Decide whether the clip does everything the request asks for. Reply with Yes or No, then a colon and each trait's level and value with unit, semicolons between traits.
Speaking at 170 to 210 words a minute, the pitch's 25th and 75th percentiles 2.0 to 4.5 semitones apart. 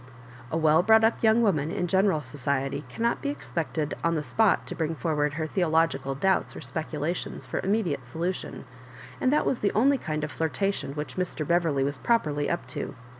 No: average, 195 wpm; average, 4.9 semitones